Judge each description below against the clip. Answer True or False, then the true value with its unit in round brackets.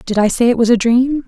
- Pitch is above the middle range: True (235 Hz)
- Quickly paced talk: True (330 wpm)